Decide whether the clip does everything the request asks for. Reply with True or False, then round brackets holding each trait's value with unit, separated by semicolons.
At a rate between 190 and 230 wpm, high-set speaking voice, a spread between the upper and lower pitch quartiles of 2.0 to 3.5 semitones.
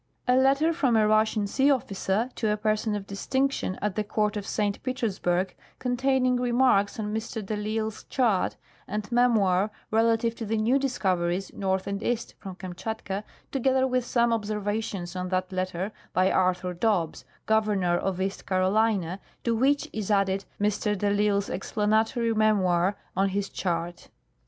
False (160 wpm; 210 Hz; 3.1 semitones)